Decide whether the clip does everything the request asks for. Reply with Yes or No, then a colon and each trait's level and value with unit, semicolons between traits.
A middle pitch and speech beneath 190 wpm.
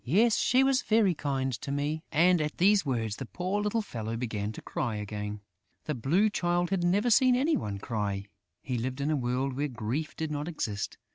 No: medium, 145 Hz; average, 200 wpm